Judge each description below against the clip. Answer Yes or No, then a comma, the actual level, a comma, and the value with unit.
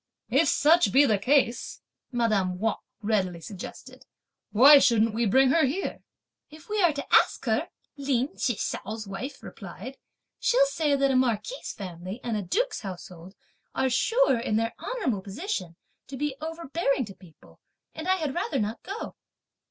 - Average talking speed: Yes, average, 160 wpm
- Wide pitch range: Yes, wide, 6.3 semitones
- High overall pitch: Yes, very high, 255 Hz